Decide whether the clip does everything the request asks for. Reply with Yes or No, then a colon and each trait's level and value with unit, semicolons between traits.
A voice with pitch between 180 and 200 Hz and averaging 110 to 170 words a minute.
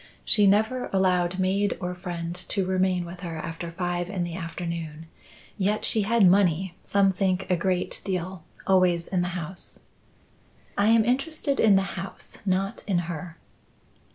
Yes: medium, 185 Hz; average, 155 wpm